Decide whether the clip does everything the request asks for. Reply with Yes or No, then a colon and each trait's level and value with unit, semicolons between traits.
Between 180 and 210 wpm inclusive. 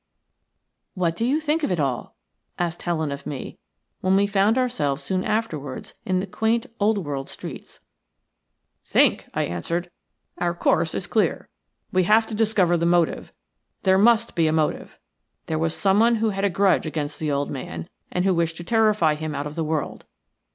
Yes: average, 185 wpm